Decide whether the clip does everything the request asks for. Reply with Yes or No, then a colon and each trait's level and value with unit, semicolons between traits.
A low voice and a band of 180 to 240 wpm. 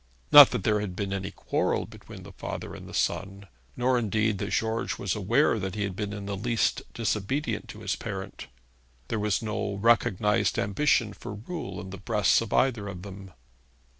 Yes: low, 105 Hz; average, 190 wpm